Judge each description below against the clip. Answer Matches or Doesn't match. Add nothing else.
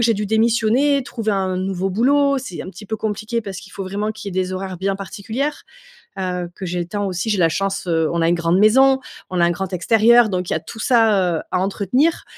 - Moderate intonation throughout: Matches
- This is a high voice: Matches